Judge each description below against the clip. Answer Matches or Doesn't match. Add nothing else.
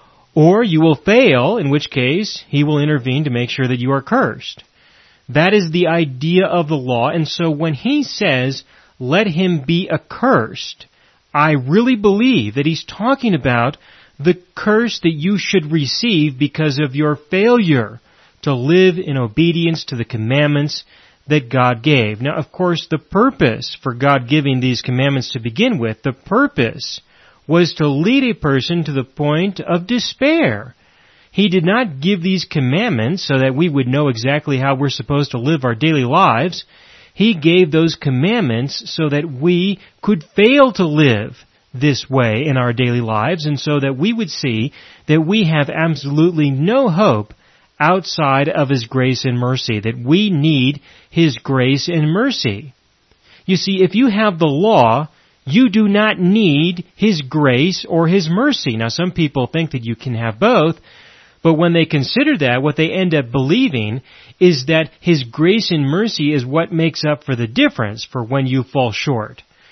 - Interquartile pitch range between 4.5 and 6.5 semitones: Matches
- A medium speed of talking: Matches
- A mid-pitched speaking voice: Matches